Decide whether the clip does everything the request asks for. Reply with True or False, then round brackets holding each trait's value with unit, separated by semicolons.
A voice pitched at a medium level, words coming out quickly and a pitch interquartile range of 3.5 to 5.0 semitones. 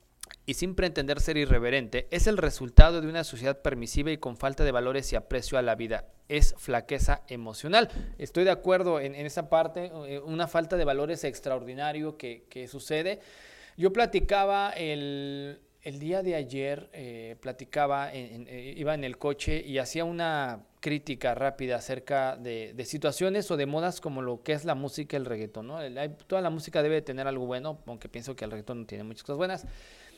True (145 Hz; 190 wpm; 4.0 semitones)